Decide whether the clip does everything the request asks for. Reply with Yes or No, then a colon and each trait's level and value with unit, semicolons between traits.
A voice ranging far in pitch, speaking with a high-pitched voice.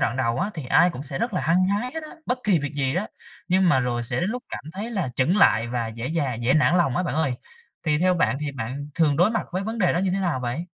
No: wide, 6.2 semitones; medium, 160 Hz